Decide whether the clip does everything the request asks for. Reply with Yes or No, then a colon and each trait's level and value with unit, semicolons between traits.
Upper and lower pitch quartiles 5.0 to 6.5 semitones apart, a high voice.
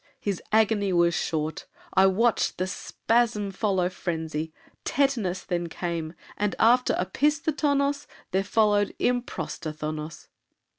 Yes: average, 5.3 semitones; high, 195 Hz